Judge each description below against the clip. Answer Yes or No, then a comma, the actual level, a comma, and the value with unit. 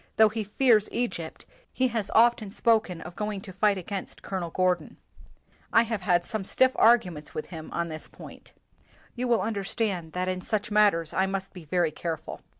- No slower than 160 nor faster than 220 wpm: Yes, average, 180 wpm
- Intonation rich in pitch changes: No, average, 3.9 semitones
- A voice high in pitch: Yes, high, 195 Hz